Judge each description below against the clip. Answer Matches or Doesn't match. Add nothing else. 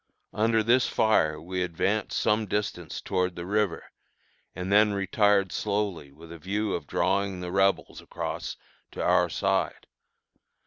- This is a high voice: Doesn't match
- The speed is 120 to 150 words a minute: Matches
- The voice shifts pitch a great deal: Doesn't match